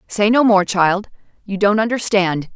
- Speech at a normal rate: Yes, average, 165 wpm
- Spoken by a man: No, female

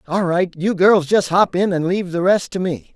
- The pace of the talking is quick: Yes, fast, 265 wpm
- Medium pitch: Yes, medium, 180 Hz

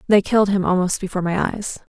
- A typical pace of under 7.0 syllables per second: Yes, 6.6 syllables/s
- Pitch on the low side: No, high, 195 Hz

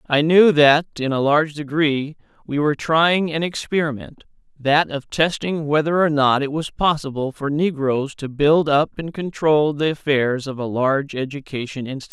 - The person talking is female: No, male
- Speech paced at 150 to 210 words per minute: Yes, average, 170 wpm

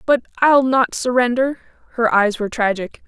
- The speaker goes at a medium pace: Yes, average, 155 wpm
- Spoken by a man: No, female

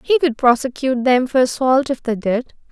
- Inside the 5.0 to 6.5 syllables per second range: Yes, 5.2 syllables/s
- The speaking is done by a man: No, female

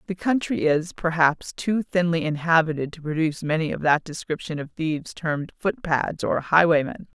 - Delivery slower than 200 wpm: Yes, average, 160 wpm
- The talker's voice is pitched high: No, medium, 165 Hz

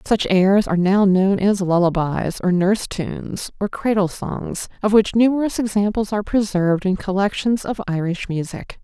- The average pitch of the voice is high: Yes, high, 195 Hz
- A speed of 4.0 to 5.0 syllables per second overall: Yes, 4.9 syllables/s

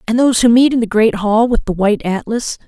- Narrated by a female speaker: No, male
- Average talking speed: No, fast, 270 wpm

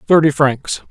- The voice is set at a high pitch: No, medium, 140 Hz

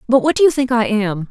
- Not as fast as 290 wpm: No, fast, 320 wpm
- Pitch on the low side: No, high, 240 Hz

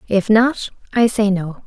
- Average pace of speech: Yes, average, 180 wpm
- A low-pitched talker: No, high, 215 Hz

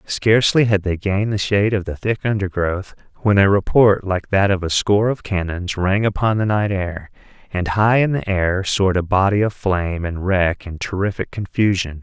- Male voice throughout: Yes, male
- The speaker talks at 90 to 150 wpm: No, average, 200 wpm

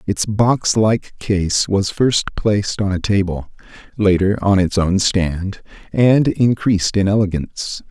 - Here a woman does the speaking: No, male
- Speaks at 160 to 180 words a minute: No, average, 145 wpm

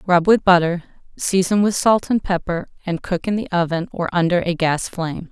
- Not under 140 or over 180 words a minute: No, fast, 205 wpm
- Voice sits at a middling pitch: Yes, medium, 180 Hz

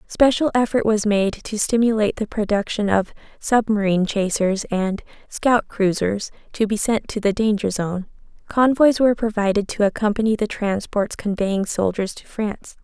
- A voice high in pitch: Yes, high, 210 Hz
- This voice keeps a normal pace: Yes, average, 150 wpm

